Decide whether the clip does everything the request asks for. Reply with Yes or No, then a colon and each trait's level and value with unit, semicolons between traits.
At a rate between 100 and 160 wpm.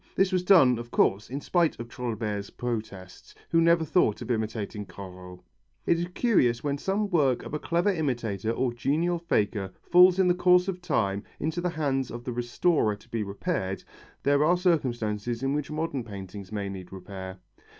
No: average, 180 wpm